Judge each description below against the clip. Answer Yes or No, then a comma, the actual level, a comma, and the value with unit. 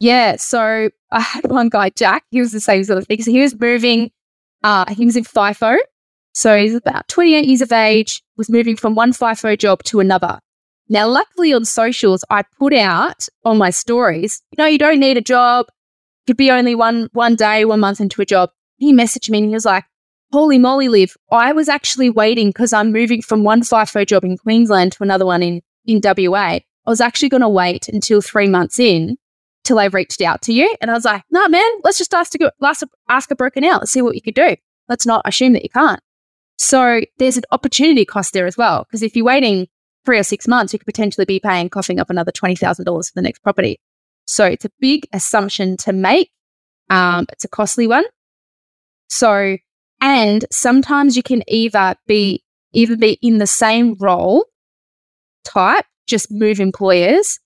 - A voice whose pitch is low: No, high, 225 Hz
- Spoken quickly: Yes, fast, 210 wpm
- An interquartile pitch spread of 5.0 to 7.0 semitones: No, average, 4.0 semitones